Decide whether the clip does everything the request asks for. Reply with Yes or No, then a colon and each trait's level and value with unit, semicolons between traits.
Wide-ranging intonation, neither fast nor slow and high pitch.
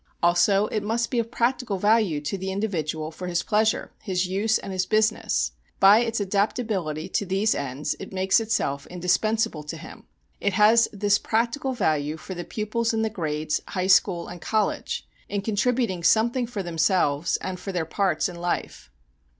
No: average, 4.1 semitones; average, 175 wpm; high, 195 Hz